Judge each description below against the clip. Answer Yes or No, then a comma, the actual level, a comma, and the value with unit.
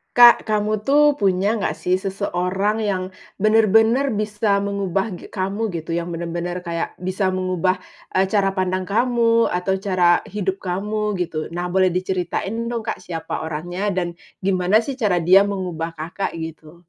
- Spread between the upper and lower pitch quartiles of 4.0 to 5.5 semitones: No, average, 3.0 semitones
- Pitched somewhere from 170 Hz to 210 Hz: Yes, high, 190 Hz